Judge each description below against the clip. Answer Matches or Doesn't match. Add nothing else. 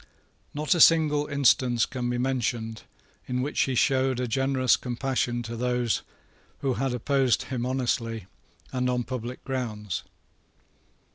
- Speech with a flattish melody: Matches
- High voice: Doesn't match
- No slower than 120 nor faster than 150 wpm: Matches